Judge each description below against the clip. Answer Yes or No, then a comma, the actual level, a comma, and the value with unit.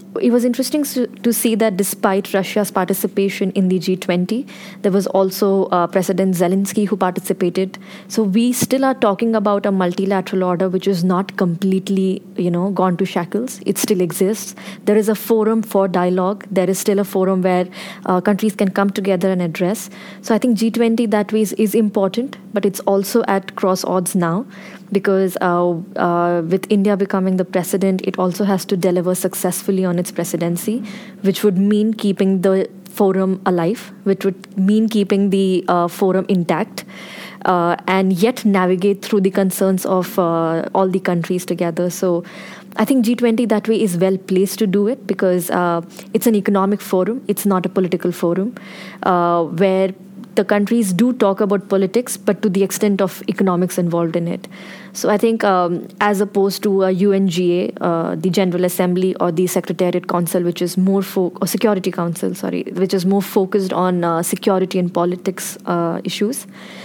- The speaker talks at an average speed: Yes, average, 175 wpm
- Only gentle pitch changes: Yes, narrow, 1.9 semitones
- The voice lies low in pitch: No, high, 195 Hz